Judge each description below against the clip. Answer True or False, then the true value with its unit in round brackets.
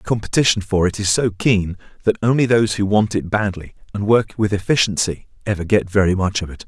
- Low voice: True (105 Hz)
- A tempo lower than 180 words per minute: False (205 wpm)